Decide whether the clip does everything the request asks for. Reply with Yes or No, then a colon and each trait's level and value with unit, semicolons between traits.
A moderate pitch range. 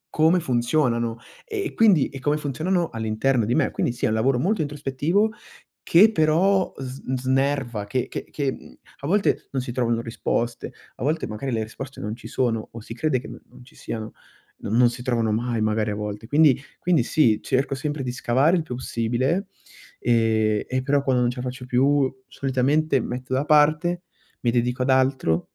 Yes: average, 4.0 semitones